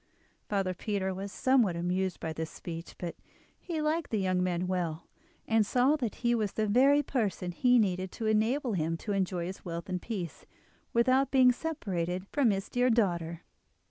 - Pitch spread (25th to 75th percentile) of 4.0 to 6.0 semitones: Yes, wide, 5.5 semitones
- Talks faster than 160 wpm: Yes, average, 175 wpm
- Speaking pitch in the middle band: No, high, 200 Hz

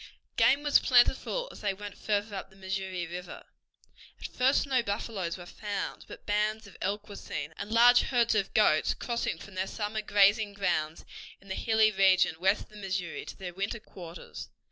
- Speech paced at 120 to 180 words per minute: No, average, 190 wpm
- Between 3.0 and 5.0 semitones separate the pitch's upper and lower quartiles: No, narrow, 2.6 semitones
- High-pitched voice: Yes, high, 200 Hz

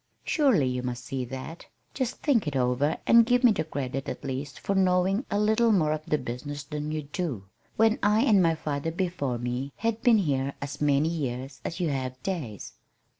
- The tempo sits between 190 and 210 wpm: Yes, average, 200 wpm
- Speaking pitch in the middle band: Yes, medium, 150 Hz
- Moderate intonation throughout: No, wide, 6.7 semitones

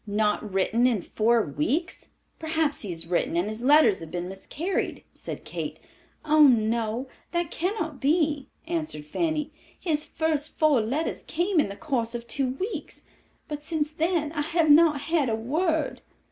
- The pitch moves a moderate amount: No, wide, 6.2 semitones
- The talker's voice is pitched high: Yes, very high, 290 Hz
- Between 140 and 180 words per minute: Yes, average, 160 wpm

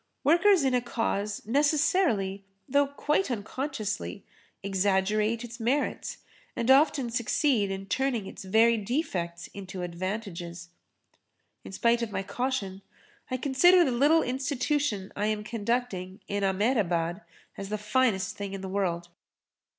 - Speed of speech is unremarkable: No, slow, 130 wpm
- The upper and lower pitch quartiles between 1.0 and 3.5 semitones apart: No, wide, 5.4 semitones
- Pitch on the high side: Yes, high, 215 Hz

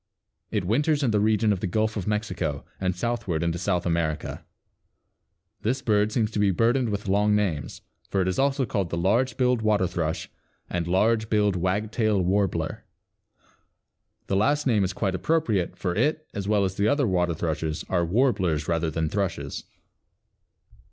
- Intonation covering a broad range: No, average, 3.9 semitones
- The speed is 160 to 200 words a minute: Yes, average, 170 wpm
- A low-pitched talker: Yes, low, 100 Hz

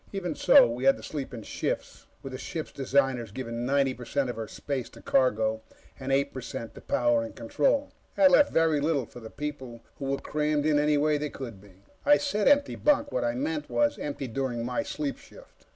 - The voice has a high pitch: No, low, 135 Hz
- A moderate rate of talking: No, fast, 220 wpm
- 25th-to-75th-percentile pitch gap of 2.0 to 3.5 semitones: No, average, 4.1 semitones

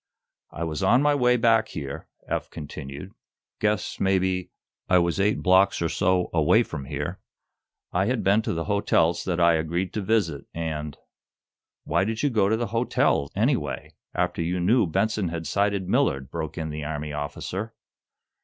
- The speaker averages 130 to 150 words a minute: No, average, 175 wpm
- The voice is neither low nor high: No, very low, 90 Hz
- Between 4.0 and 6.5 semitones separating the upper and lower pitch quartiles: Yes, average, 4.8 semitones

